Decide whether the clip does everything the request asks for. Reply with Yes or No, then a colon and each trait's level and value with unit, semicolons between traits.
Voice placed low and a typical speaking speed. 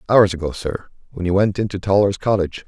Yes: very low, 95 Hz; average, 180 wpm